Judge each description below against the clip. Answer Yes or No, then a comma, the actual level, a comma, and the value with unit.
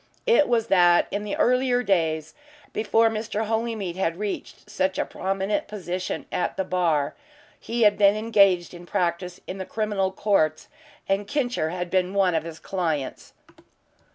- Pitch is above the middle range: Yes, high, 195 Hz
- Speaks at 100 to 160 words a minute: Yes, average, 155 wpm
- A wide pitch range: No, average, 3.3 semitones